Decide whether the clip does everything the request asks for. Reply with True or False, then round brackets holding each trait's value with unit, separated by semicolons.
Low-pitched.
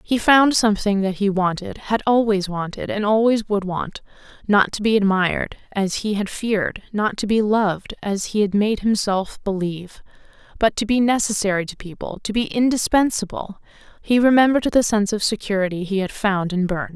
False (205 Hz)